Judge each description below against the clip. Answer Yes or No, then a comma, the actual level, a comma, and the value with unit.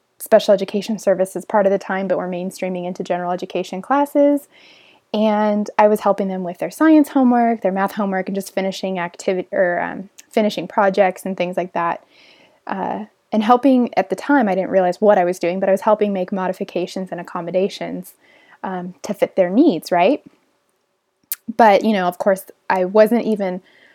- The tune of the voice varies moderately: Yes, average, 3.0 semitones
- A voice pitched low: No, high, 195 Hz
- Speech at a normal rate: Yes, average, 185 wpm